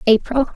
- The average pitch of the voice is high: Yes, high, 245 Hz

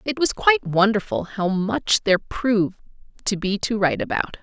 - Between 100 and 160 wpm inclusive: No, average, 175 wpm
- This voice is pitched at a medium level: No, high, 210 Hz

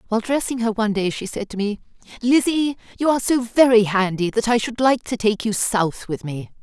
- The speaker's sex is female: Yes, female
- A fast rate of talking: Yes, fast, 225 wpm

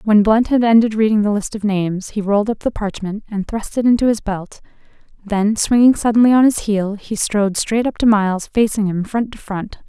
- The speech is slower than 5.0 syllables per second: No, 5.4 syllables/s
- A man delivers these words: No, female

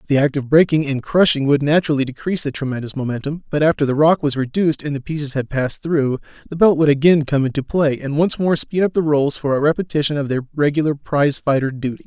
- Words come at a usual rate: No, fast, 235 wpm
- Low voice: No, medium, 145 Hz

